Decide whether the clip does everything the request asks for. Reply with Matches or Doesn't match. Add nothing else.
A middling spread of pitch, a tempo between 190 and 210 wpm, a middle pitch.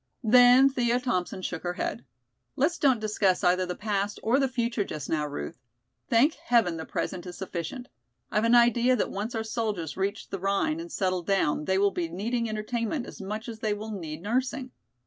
Doesn't match